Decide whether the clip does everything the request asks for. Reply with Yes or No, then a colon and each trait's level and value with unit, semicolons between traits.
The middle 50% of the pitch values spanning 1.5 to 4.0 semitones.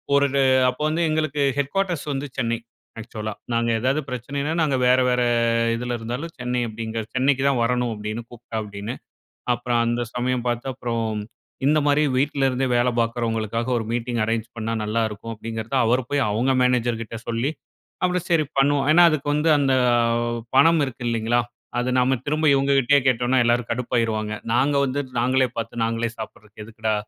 Yes: average, 3.1 semitones